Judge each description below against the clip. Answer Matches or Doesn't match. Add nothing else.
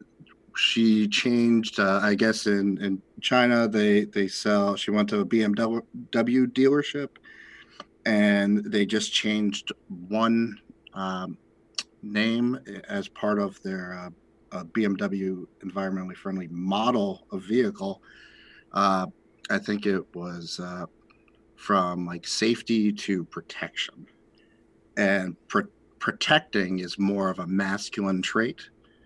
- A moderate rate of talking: Doesn't match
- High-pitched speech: Doesn't match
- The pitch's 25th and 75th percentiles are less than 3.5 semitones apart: Matches